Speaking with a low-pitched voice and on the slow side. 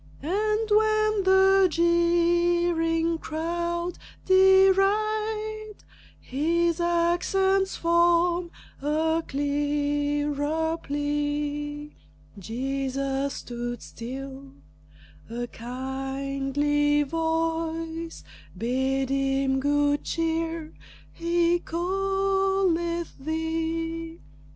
No: very high, 325 Hz; slow, 60 wpm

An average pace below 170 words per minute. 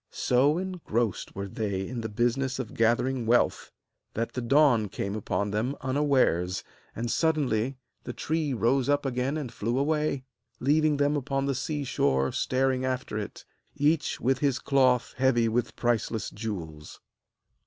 Yes: average, 150 wpm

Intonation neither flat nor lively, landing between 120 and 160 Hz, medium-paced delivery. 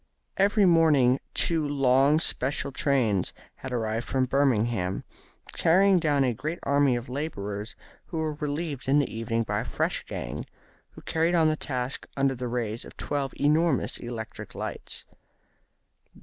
Yes: average, 4.3 semitones; low, 135 Hz; average, 150 wpm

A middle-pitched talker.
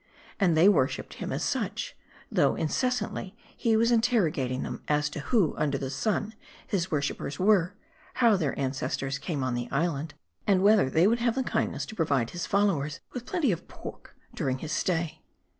Yes: medium, 170 Hz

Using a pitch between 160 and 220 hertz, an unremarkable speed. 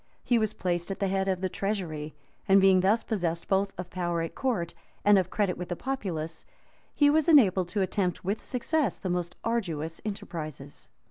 Yes: high, 190 Hz; average, 190 wpm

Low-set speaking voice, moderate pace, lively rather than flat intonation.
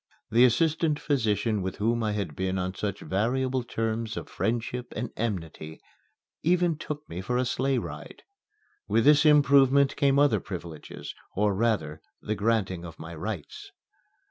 Yes: low, 115 Hz; average, 150 wpm; wide, 6.0 semitones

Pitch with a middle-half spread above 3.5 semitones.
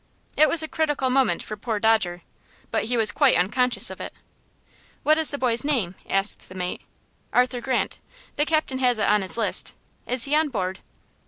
Yes: average, 5.2 semitones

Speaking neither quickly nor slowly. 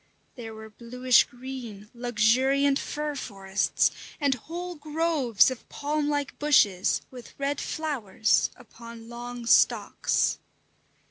No: slow, 110 wpm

